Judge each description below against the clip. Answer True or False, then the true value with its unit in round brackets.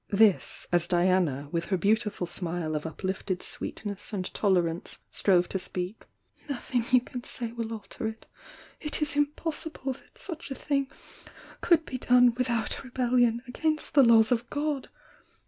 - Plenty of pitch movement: True (5.8 semitones)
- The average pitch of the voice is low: False (230 Hz)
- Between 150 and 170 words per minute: True (160 wpm)